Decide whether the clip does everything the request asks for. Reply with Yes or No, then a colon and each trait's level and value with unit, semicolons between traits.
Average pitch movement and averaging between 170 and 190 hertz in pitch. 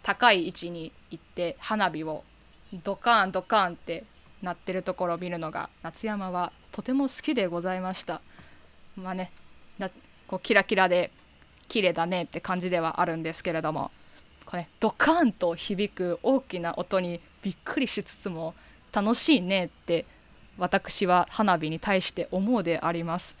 Yes: average, 3.2 semitones; medium, 185 Hz